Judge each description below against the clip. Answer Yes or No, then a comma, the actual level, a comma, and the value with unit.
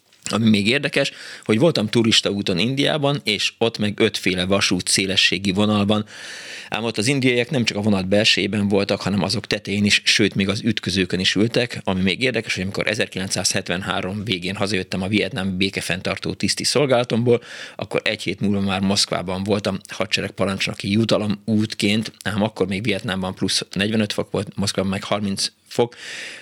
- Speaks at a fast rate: Yes, fast, 160 wpm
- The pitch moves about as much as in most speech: No, narrow, 2.2 semitones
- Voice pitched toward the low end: Yes, low, 100 Hz